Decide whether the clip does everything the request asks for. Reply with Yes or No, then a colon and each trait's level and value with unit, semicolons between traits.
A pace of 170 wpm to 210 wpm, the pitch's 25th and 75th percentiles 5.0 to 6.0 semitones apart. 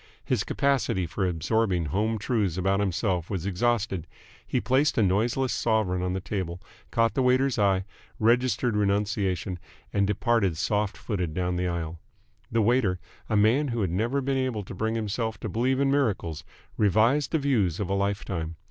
No: average, 175 wpm; average, 4.3 semitones